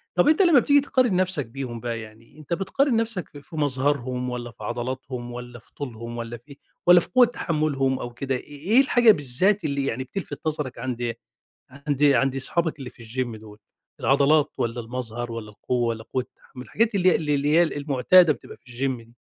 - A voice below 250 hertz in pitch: Yes, low, 135 Hz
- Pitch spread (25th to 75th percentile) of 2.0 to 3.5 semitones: No, average, 4.9 semitones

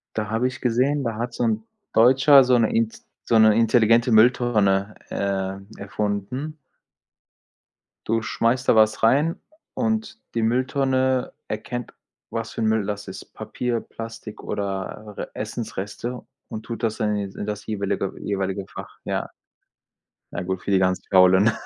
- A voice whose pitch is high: No, low, 110 Hz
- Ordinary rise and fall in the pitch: Yes, average, 3.4 semitones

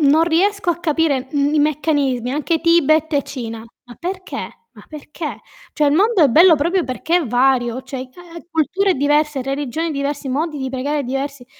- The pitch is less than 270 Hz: No, very high, 295 Hz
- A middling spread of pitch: Yes, average, 3.4 semitones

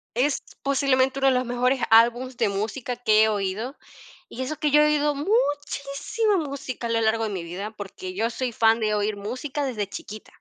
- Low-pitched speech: No, high, 245 Hz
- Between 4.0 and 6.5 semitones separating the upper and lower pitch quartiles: Yes, average, 4.3 semitones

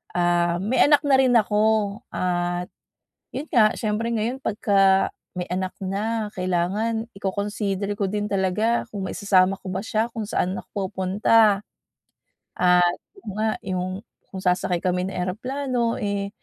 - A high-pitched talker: Yes, high, 200 Hz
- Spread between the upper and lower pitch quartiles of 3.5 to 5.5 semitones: No, average, 3.0 semitones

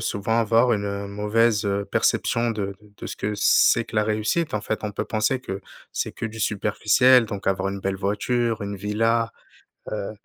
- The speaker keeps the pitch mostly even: Yes, narrow, 2.2 semitones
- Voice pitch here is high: No, low, 105 Hz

